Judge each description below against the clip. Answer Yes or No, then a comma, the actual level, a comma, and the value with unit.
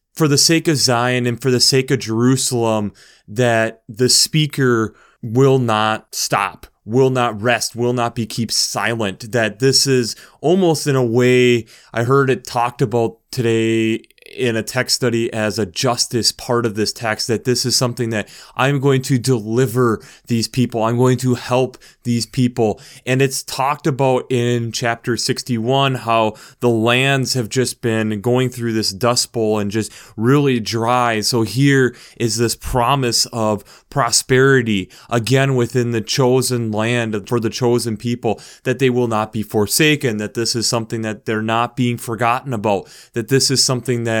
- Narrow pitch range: Yes, narrow, 2.3 semitones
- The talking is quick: No, average, 170 wpm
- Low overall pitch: Yes, low, 120 Hz